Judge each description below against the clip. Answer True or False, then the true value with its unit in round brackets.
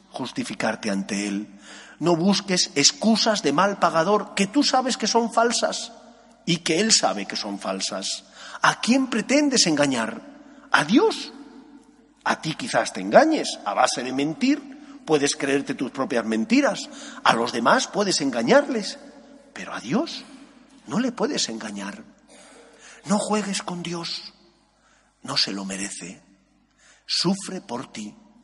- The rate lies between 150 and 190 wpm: False (135 wpm)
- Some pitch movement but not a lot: False (8.9 semitones)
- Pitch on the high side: True (220 Hz)